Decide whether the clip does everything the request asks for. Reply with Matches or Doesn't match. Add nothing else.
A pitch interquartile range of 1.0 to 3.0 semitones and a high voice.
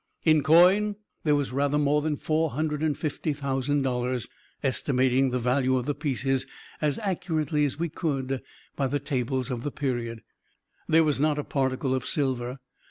Doesn't match